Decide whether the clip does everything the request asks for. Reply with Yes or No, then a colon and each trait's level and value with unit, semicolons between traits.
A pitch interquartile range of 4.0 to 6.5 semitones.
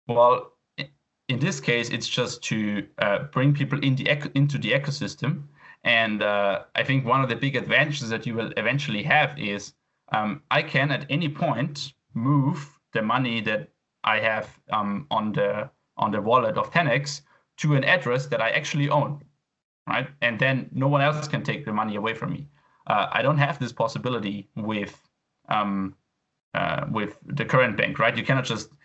Yes: average, 4.4 semitones